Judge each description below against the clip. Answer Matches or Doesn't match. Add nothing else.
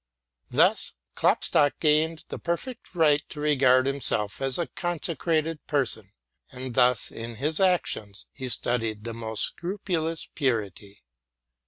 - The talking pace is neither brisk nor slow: Doesn't match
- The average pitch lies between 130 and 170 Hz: Matches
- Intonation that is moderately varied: Doesn't match